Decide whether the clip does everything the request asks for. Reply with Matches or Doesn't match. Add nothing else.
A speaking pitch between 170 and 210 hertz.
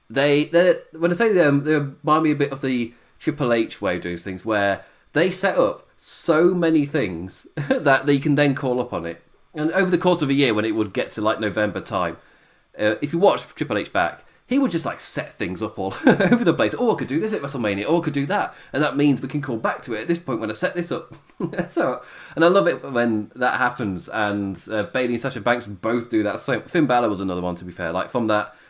Doesn't match